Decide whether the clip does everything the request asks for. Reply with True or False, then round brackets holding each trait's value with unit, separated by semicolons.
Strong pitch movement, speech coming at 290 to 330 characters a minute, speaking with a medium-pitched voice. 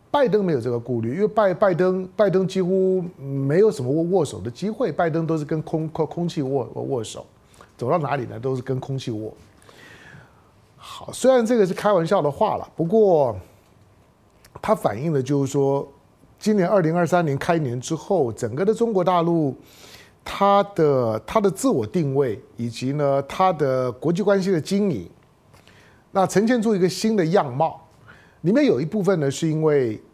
False (6.1 semitones; 255 characters per minute; 160 Hz)